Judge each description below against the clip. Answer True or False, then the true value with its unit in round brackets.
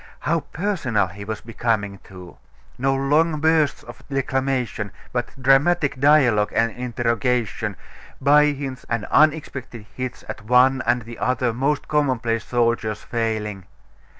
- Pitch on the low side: True (125 Hz)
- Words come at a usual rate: False (125 wpm)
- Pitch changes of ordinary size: True (3.6 semitones)